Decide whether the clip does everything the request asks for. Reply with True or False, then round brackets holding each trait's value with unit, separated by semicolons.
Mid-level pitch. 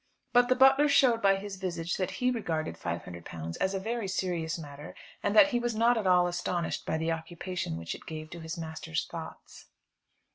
True (180 Hz)